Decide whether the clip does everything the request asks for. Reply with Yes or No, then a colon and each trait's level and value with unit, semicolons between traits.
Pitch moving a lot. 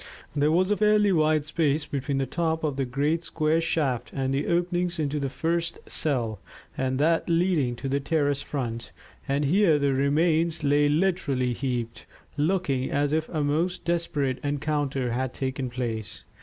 No: average, 3.5 semitones